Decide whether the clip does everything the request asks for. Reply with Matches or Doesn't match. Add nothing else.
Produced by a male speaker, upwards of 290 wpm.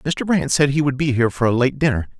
Matches